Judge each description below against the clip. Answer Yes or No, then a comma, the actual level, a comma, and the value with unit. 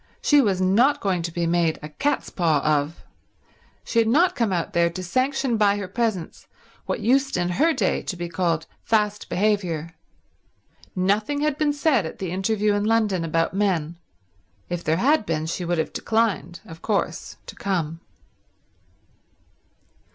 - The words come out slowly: No, average, 165 wpm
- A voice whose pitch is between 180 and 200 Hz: Yes, high, 190 Hz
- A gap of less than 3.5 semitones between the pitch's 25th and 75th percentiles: No, average, 5.1 semitones